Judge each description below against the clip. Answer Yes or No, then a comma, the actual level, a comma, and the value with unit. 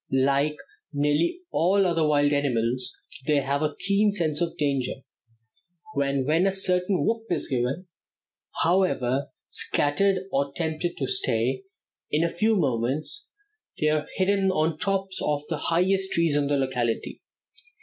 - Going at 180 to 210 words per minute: No, average, 145 wpm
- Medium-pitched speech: Yes, medium, 155 Hz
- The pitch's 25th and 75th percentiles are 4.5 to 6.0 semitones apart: Yes, average, 4.9 semitones